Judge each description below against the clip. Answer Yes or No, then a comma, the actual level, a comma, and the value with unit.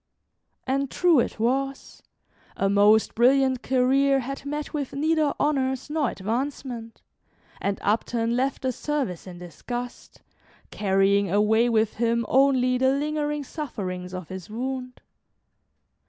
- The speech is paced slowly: Yes, slow, 125 wpm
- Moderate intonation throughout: Yes, average, 4.1 semitones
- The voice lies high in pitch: Yes, very high, 250 Hz